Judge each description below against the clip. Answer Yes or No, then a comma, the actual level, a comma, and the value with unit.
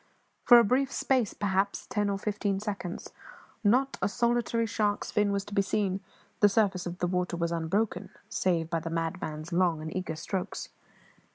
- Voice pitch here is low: No, high, 195 Hz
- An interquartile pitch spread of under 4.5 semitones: Yes, average, 3.1 semitones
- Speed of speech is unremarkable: Yes, average, 175 wpm